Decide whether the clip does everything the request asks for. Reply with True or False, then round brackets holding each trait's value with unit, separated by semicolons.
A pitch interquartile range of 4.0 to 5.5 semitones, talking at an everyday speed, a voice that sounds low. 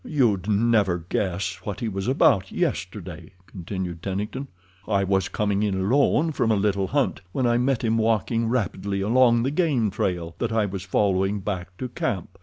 False (3.6 semitones; 175 wpm; 105 Hz)